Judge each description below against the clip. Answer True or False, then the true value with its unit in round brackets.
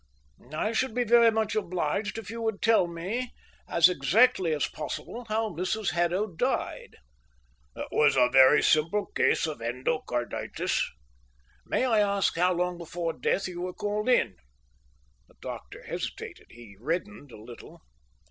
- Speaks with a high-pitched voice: False (180 Hz)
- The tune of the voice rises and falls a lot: True (5.8 semitones)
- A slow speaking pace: False (145 wpm)